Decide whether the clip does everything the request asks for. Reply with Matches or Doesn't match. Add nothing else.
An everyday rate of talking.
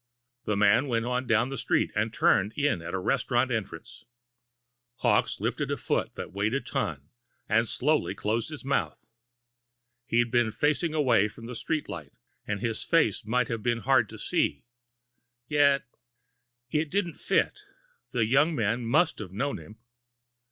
Matches